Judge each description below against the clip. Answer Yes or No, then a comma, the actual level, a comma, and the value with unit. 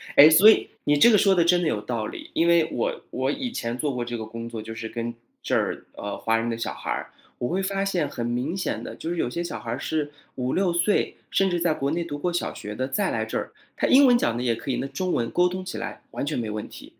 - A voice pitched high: No, medium, 150 Hz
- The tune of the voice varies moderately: No, wide, 7.3 semitones